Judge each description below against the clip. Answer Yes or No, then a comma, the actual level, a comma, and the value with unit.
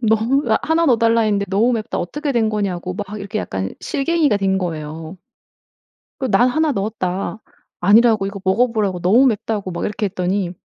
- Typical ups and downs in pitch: Yes, average, 3.9 semitones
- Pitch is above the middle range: Yes, high, 210 Hz